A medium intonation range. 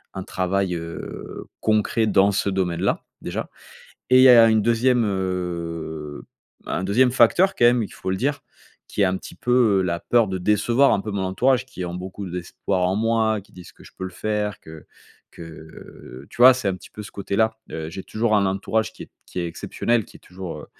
Yes: average, 3.8 semitones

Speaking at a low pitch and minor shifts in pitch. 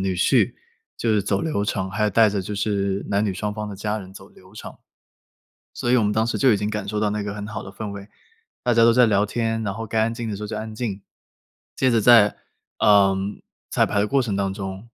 Yes: low, 105 Hz; narrow, 2.1 semitones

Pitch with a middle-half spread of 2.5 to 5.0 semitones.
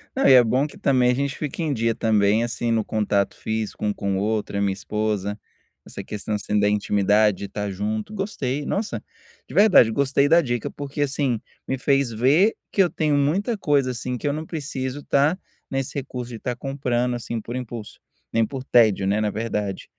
Yes: average, 4.7 semitones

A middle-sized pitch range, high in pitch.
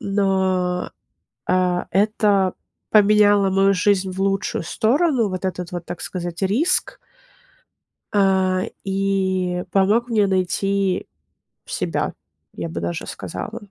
No: narrow, 1.8 semitones; high, 195 Hz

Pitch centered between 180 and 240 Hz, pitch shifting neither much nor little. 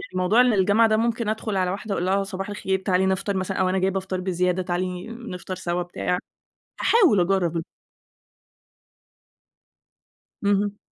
No: high, 190 Hz; narrow, 2.1 semitones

